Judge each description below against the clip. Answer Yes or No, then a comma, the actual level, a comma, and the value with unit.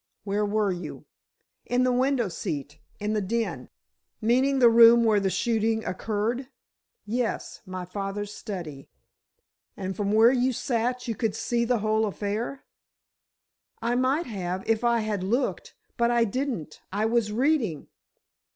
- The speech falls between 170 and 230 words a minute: No, slow, 135 wpm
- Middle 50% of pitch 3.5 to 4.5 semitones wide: No, average, 3.0 semitones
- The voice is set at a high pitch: Yes, high, 220 Hz